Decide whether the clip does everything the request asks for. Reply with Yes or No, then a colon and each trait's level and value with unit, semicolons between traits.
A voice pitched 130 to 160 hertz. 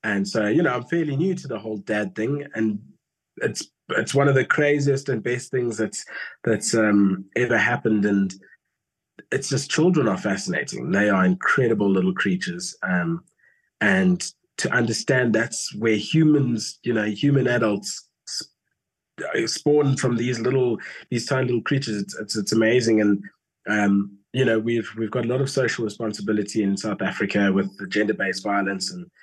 No: low, 115 Hz